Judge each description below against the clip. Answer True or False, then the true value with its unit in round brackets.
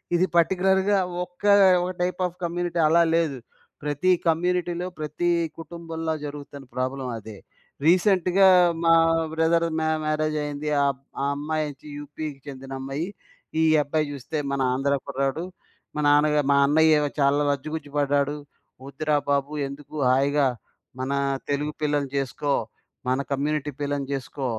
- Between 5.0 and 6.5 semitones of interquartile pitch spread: False (2.9 semitones)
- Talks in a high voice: False (150 Hz)